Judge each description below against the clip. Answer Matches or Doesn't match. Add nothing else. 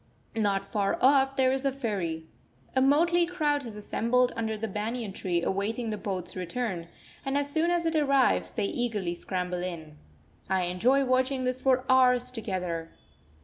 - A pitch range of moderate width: Doesn't match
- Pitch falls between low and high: Doesn't match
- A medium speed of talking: Matches